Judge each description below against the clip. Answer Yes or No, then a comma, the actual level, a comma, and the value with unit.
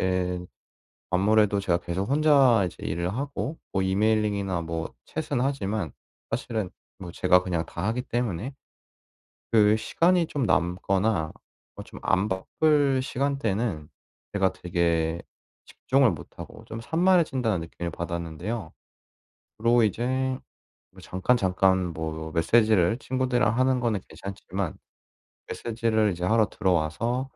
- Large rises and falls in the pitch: Yes, wide, 5.7 semitones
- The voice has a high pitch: No, low, 105 Hz